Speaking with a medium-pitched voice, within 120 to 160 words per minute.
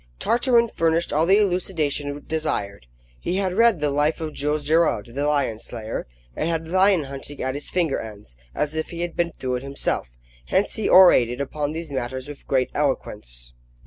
No: medium, 150 Hz; average, 180 wpm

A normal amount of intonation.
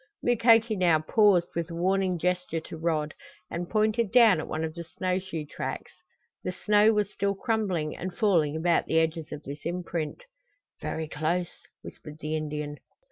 Yes: average, 4.0 semitones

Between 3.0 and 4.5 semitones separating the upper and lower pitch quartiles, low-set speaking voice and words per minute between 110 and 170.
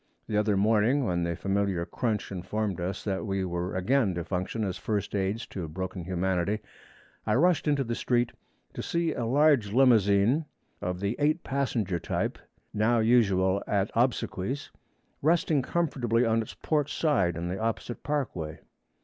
No: average, 5.2 semitones; low, 105 Hz; average, 160 wpm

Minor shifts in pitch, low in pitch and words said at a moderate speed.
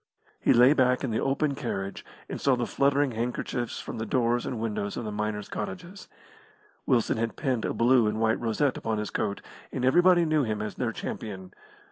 No: average, 3.8 semitones; low, 120 Hz; average, 195 wpm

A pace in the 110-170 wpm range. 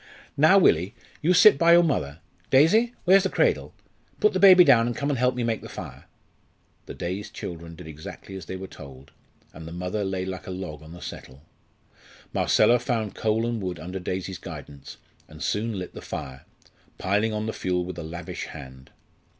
No: average, 195 wpm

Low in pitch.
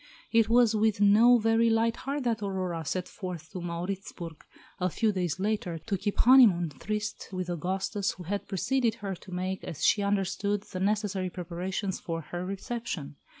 No: high, 195 Hz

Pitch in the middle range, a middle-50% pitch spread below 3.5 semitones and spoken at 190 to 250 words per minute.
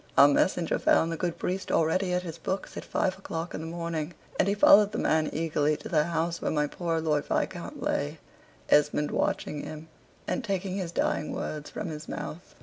Yes: medium, 165 Hz; average, 2.8 semitones; average, 200 wpm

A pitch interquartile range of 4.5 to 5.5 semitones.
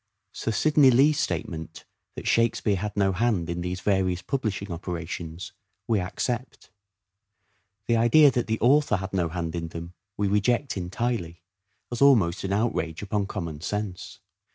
Yes: average, 5.1 semitones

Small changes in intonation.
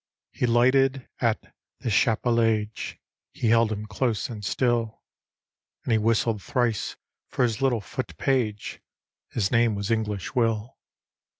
Yes: narrow, 2.2 semitones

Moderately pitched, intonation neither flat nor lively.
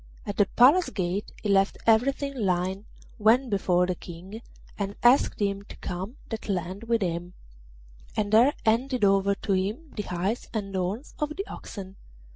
No: high, 205 Hz; average, 3.6 semitones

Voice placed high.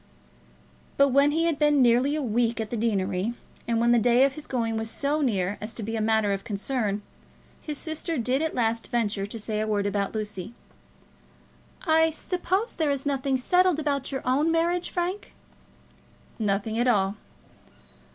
Yes: high, 240 Hz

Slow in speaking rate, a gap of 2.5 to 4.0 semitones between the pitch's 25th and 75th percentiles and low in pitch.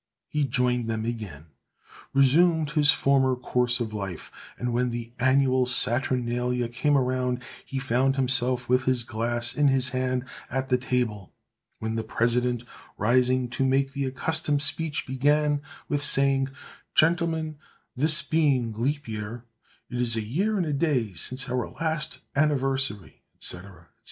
No: average, 145 wpm; average, 2.9 semitones; low, 130 Hz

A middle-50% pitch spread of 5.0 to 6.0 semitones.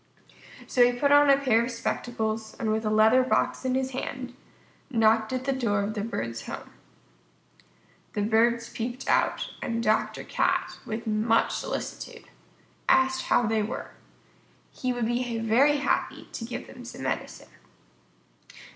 No: average, 2.7 semitones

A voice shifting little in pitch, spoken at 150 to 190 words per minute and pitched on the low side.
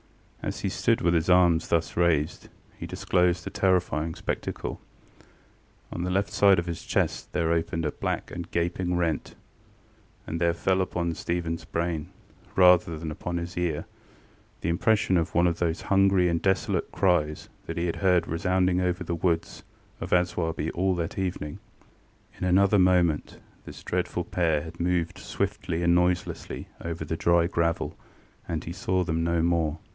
Yes: narrow, 1.5 semitones; average, 165 wpm; very low, 85 Hz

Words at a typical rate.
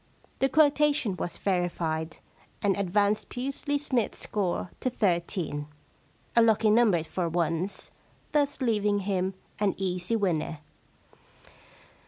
No: slow, 120 wpm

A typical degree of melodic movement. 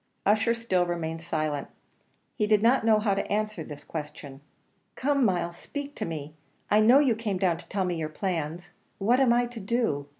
No: wide, 5.8 semitones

